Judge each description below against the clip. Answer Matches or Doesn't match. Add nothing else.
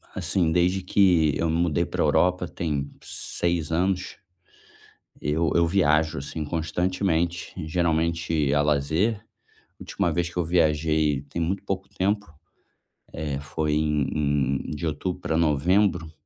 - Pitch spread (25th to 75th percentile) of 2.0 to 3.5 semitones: Matches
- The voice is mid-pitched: Doesn't match